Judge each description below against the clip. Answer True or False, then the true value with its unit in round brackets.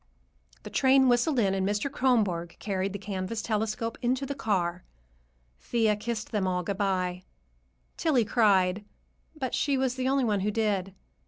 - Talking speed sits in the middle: True (160 wpm)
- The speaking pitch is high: True (215 Hz)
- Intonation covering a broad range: False (4.5 semitones)